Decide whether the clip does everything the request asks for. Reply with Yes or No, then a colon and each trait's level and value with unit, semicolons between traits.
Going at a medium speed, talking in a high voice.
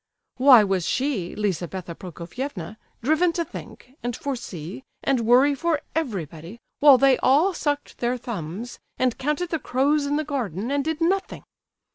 Yes: average, 150 wpm; very high, 255 Hz